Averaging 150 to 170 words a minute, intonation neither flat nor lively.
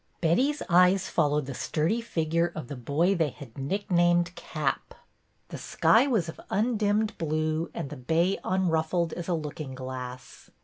Yes: average, 160 wpm; average, 3.8 semitones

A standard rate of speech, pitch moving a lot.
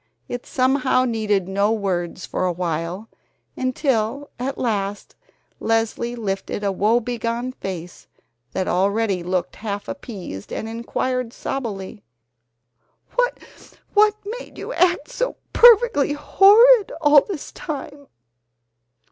No: slow, 105 wpm; wide, 6.3 semitones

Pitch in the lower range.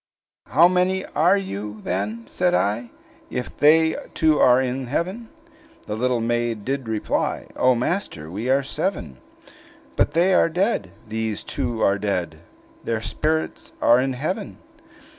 Yes: low, 125 Hz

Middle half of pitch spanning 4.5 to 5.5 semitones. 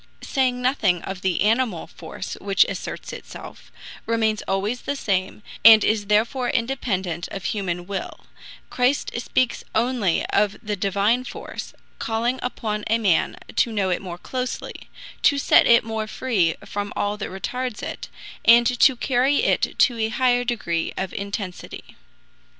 No: average, 4.1 semitones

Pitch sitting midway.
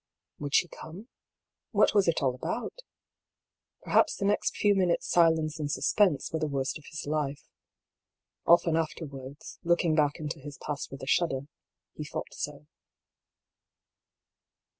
Yes: medium, 155 Hz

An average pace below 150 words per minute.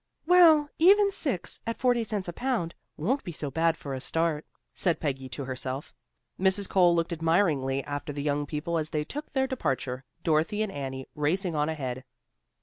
No: average, 180 wpm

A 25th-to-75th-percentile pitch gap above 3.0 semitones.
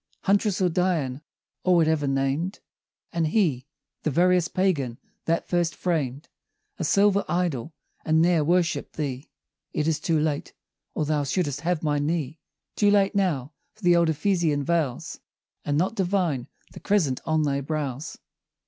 Yes: average, 3.8 semitones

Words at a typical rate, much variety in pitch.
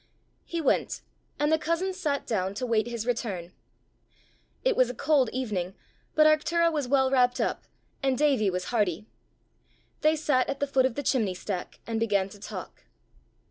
Yes: average, 175 wpm; wide, 5.9 semitones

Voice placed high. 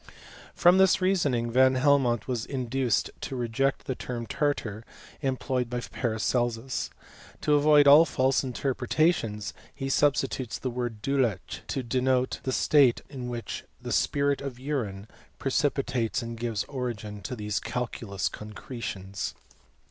No: low, 125 Hz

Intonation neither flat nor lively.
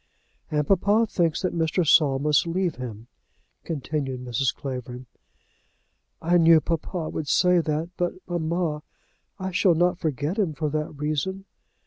Yes: average, 3.3 semitones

